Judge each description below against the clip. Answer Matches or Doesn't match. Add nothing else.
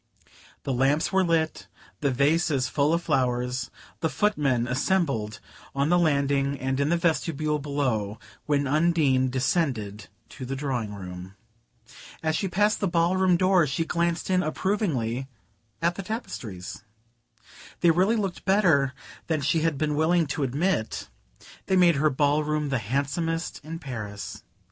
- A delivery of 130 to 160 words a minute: Matches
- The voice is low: Doesn't match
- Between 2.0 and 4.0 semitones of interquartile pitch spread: Doesn't match